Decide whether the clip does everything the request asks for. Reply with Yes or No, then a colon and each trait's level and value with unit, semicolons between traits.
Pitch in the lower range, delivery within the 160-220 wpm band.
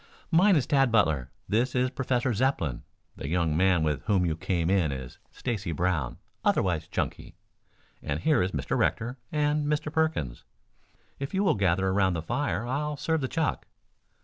Yes: low, 100 Hz; average, 170 wpm